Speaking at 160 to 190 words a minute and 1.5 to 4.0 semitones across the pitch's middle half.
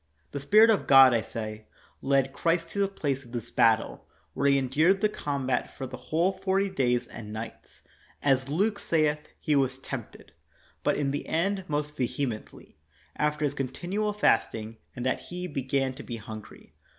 No: average, 180 wpm; average, 5.1 semitones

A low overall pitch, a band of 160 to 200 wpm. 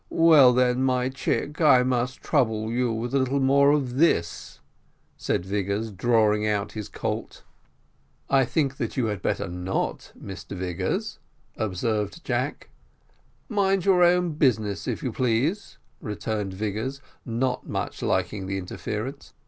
No: low, 120 Hz; average, 140 wpm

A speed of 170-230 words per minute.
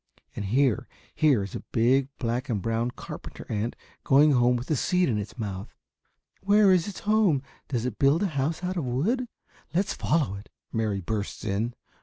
Yes: average, 185 wpm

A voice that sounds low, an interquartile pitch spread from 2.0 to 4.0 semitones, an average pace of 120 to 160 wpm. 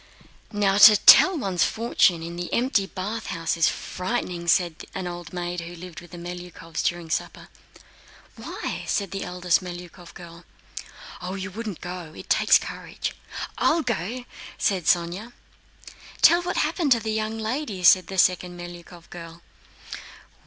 No: medium, 180 Hz; average, 3.7 semitones; average, 145 wpm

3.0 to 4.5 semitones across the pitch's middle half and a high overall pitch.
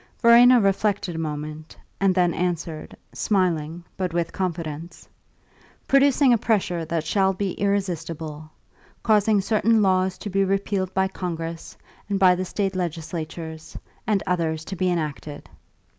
No: average, 3.3 semitones; medium, 180 Hz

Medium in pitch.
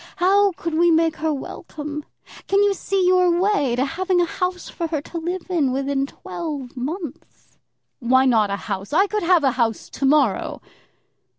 No: very high, 320 Hz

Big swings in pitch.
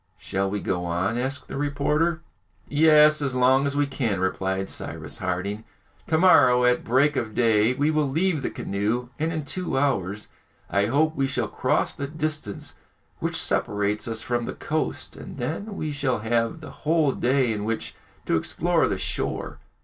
Yes: wide, 5.8 semitones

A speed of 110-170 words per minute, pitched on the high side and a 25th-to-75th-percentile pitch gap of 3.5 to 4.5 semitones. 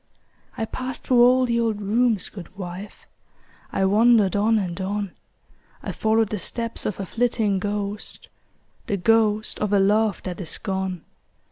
No: average, 155 wpm; high, 210 Hz; average, 2.7 semitones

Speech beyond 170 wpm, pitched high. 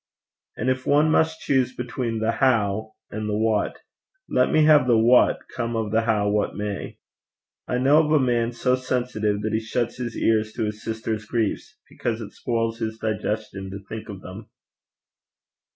No: average, 180 wpm; low, 115 Hz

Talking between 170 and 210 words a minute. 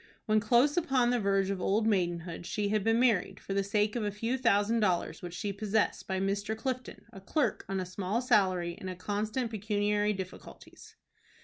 Yes: average, 190 wpm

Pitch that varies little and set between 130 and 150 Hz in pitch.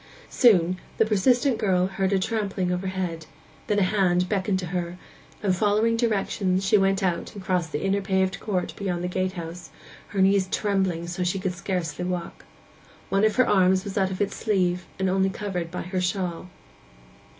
No: narrow, 1.8 semitones; high, 190 Hz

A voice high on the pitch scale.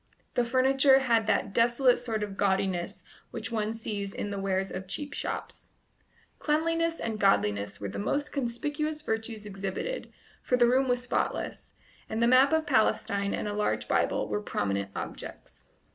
Yes: high, 225 Hz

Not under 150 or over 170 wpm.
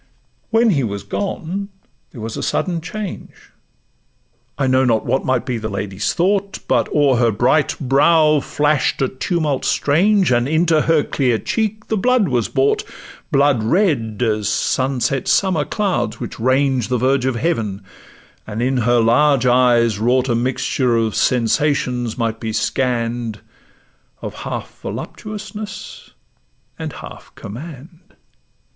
No: average, 140 wpm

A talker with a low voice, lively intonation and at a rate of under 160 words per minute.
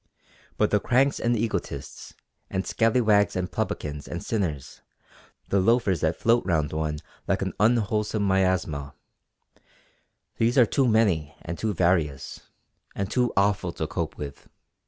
Yes: very low, 95 Hz; wide, 5.9 semitones; slow, 135 wpm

